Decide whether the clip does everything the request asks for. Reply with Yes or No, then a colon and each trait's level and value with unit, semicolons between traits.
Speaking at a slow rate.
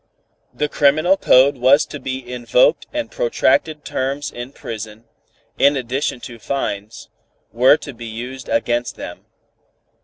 Yes: slow, 130 wpm